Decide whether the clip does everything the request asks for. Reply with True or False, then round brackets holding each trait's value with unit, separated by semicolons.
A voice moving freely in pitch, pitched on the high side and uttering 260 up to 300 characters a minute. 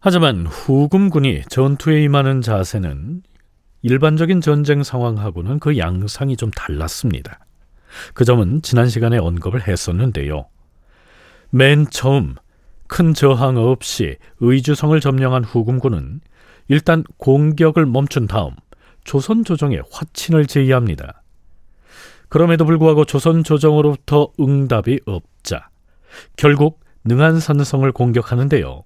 False (6.0 semitones; 135 Hz; 265 characters per minute)